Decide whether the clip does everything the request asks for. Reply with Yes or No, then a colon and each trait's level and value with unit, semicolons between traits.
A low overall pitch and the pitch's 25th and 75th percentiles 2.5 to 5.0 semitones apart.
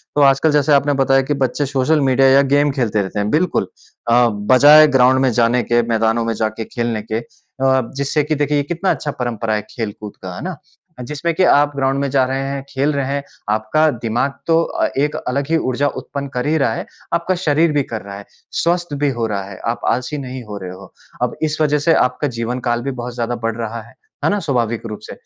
Yes: low, 130 Hz; average, 4.0 semitones